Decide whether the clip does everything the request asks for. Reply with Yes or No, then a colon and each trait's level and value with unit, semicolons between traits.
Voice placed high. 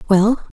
Yes: high, 210 Hz